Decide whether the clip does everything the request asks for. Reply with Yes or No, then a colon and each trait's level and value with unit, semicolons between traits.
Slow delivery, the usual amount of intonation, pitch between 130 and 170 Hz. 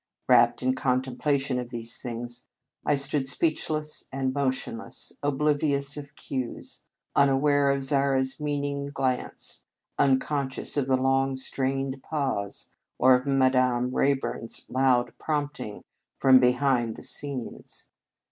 No: slow, 130 wpm; narrow, 1.7 semitones; low, 135 Hz